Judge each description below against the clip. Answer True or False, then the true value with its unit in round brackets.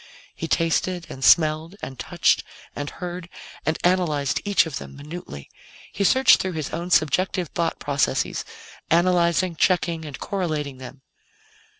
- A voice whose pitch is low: False (165 Hz)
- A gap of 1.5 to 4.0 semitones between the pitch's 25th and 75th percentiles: True (3.5 semitones)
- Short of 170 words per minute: True (135 wpm)